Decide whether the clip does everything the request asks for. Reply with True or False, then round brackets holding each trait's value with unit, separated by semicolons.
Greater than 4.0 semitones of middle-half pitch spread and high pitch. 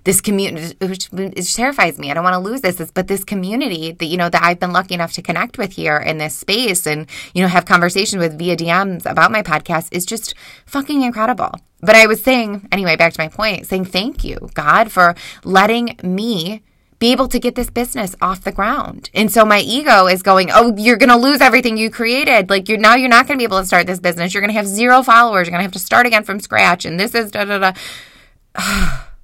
True (4.4 semitones; 195 Hz)